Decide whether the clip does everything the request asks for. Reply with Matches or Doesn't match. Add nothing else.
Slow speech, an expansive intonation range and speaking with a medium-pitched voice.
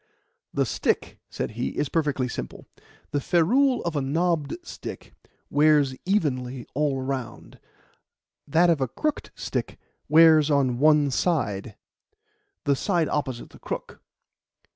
Doesn't match